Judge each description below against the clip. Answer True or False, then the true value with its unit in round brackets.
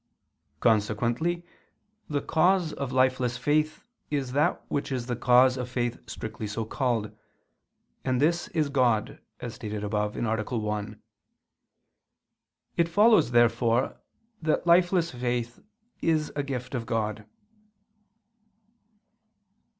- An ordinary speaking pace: False (110 wpm)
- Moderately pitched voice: False (125 Hz)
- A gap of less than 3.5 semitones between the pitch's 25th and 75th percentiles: False (4.8 semitones)